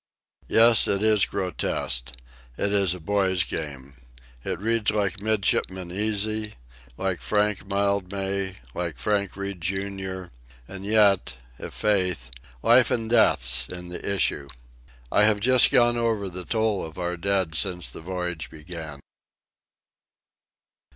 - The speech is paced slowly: Yes, slow, 130 wpm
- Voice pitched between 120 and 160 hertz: No, very low, 95 Hz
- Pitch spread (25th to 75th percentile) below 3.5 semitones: Yes, average, 3.0 semitones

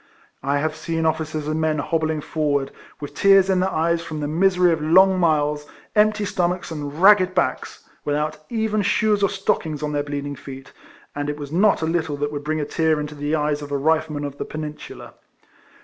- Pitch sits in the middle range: Yes, medium, 155 Hz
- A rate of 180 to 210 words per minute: Yes, fast, 205 wpm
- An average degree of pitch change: Yes, average, 3.5 semitones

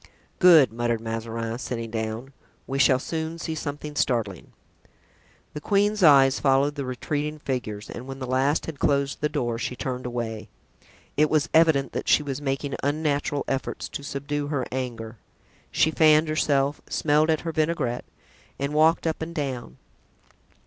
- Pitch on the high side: No, medium, 140 Hz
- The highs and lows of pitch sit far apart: No, average, 3.7 semitones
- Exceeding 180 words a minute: No, average, 155 wpm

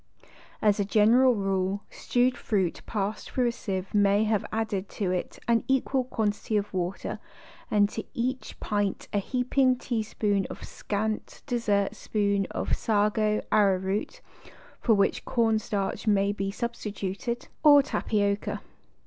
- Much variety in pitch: No, average, 2.8 semitones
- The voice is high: Yes, high, 210 Hz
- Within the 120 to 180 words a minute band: Yes, average, 140 wpm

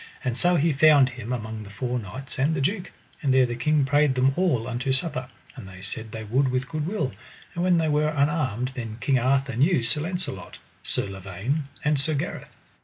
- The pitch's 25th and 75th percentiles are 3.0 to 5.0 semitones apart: Yes, average, 4.0 semitones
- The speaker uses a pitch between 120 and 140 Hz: Yes, low, 135 Hz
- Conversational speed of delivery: No, fast, 210 wpm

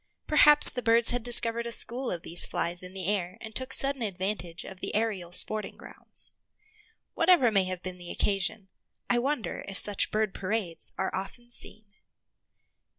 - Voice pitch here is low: No, high, 210 Hz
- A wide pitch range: No, average, 4.4 semitones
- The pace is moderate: Yes, average, 170 wpm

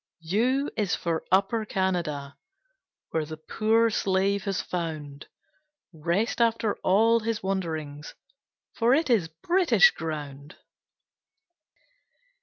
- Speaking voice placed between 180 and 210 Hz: Yes, high, 190 Hz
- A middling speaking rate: No, slow, 105 wpm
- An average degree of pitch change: No, wide, 5.9 semitones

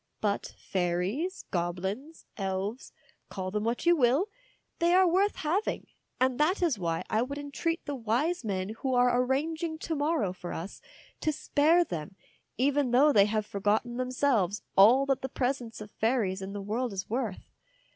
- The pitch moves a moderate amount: No, wide, 6.5 semitones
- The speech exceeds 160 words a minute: Yes, average, 170 wpm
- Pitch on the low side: No, high, 245 Hz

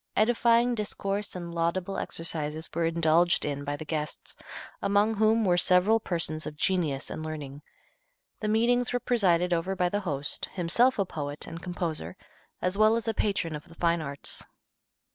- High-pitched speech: No, medium, 175 Hz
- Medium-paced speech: Yes, average, 165 wpm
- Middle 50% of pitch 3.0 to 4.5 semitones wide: No, average, 4.9 semitones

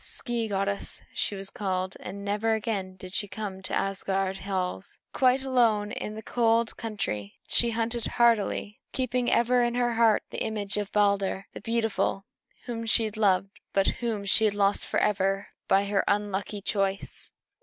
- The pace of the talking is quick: No, average, 160 wpm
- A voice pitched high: Yes, high, 205 Hz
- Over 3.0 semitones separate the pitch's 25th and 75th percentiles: No, average, 2.7 semitones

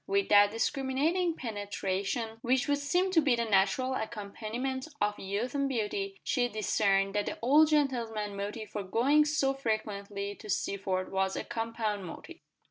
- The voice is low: No, high, 225 Hz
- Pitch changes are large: No, average, 4.9 semitones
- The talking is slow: No, average, 155 wpm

